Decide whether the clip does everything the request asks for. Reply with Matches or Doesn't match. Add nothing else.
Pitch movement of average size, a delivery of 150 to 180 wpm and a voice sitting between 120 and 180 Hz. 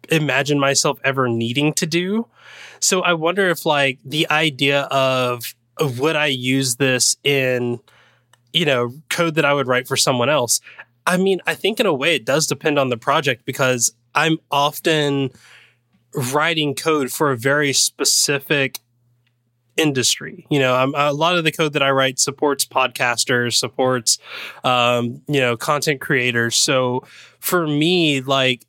Matches